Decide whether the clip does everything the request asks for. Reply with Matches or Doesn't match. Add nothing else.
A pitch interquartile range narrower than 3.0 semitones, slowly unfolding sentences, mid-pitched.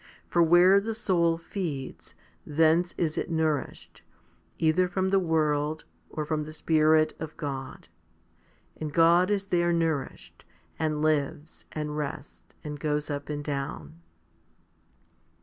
Matches